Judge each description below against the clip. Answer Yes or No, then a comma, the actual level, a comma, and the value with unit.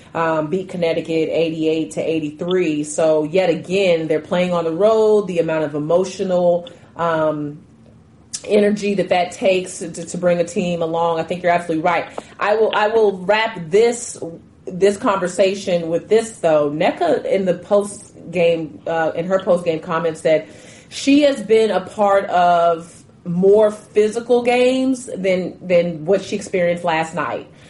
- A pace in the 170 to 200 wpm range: No, average, 155 wpm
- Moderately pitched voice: Yes, medium, 175 Hz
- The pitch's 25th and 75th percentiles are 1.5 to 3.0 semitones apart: No, average, 3.5 semitones